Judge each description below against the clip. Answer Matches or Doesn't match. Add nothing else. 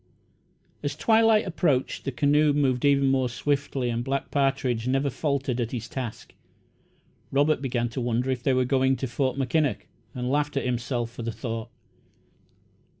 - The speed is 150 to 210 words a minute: Matches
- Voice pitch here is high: Doesn't match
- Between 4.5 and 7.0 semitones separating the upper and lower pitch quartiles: Doesn't match